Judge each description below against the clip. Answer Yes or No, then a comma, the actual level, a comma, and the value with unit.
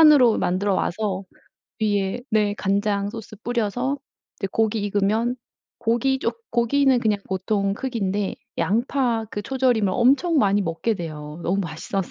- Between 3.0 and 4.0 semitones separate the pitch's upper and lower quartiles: Yes, average, 3.6 semitones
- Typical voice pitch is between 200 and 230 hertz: Yes, high, 210 Hz